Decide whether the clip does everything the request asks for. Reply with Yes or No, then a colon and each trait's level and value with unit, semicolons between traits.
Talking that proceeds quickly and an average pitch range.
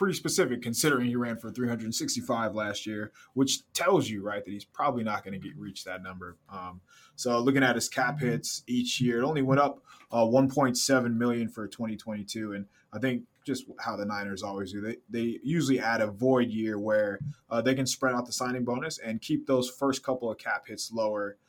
Yes: fast, 215 wpm; average, 3.4 semitones